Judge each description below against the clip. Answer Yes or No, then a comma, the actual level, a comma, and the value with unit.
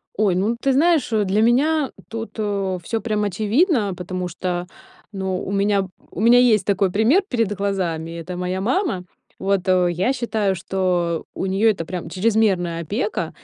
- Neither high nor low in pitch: No, high, 200 Hz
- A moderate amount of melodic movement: Yes, average, 3.6 semitones